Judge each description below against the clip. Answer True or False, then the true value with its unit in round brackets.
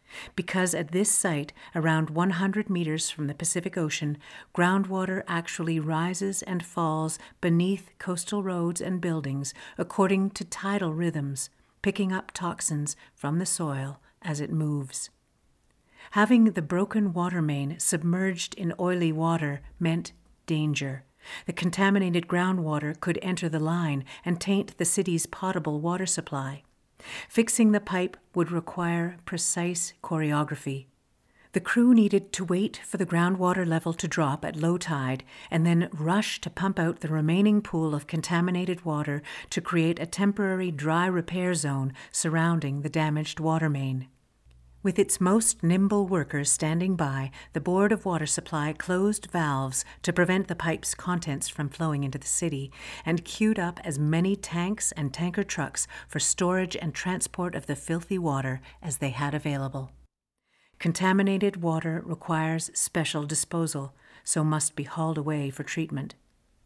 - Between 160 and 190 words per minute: False (145 wpm)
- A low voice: False (170 Hz)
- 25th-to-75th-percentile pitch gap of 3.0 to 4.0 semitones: True (3.3 semitones)